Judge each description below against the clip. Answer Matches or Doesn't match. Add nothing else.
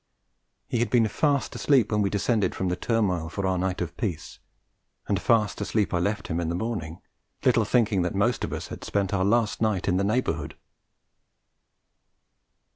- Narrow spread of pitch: Doesn't match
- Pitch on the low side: Matches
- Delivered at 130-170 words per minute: Doesn't match